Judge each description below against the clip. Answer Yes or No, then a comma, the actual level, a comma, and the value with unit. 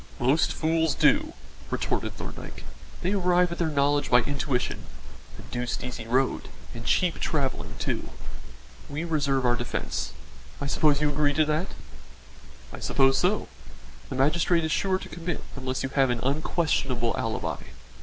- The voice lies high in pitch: No, medium, 145 Hz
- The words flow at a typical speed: Yes, average, 150 wpm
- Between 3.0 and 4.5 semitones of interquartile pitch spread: Yes, average, 4.1 semitones